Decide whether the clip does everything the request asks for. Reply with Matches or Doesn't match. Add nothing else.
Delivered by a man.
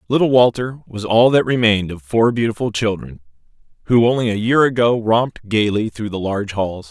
Matches